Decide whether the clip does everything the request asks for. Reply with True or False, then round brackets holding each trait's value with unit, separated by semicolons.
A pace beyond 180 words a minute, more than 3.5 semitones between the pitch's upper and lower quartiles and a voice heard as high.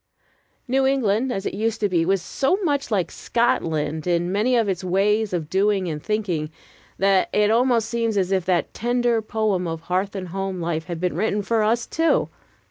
True (195 wpm; 4.1 semitones; 200 Hz)